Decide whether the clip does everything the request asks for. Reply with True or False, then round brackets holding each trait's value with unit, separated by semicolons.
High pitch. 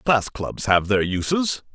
False (120 Hz)